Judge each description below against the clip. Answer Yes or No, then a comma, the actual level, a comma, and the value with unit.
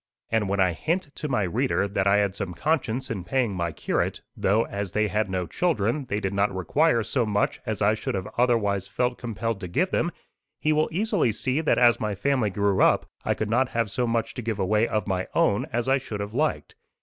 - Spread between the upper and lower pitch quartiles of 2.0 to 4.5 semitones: Yes, average, 4.0 semitones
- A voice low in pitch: Yes, low, 110 Hz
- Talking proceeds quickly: Yes, fast, 230 wpm